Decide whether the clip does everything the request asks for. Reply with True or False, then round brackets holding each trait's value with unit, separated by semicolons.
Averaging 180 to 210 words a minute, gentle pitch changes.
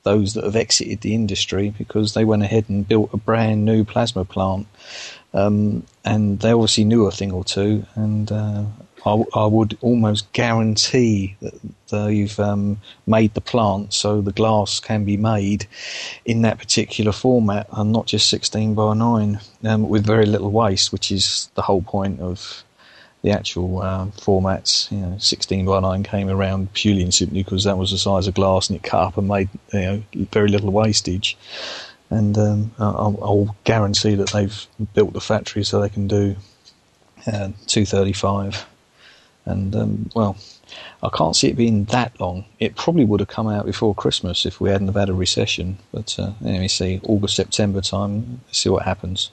True (185 wpm; 1.8 semitones)